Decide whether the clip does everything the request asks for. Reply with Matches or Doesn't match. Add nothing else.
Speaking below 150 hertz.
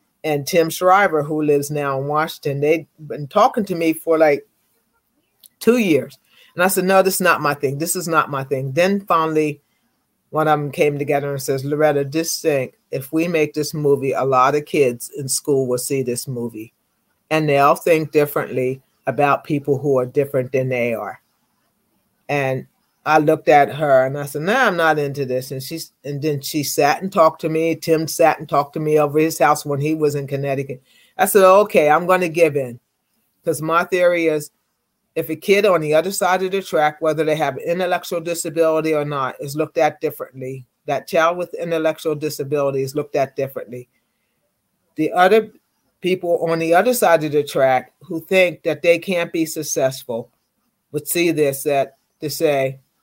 Doesn't match